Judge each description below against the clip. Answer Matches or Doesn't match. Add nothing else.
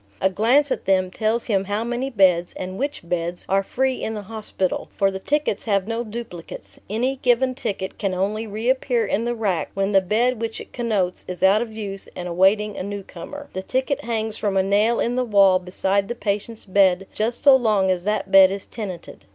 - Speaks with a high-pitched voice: Matches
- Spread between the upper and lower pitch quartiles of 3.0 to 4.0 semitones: Matches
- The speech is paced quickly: Matches